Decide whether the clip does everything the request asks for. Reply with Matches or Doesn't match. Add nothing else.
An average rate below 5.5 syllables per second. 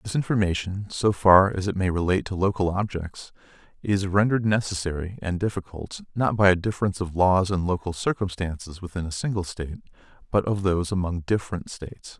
Doesn't match